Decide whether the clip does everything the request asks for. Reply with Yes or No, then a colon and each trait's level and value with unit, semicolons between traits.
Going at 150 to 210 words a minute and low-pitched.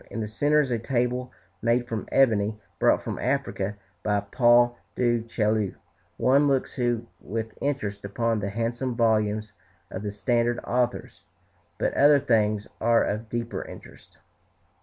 No: average, 140 wpm; low, 115 Hz